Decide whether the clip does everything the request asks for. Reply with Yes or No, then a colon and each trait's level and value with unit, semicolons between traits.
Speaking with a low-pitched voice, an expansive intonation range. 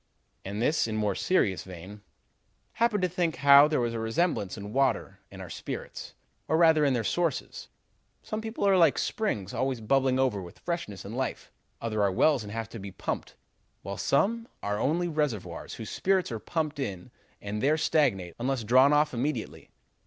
Yes: low, 130 Hz; wide, 7.1 semitones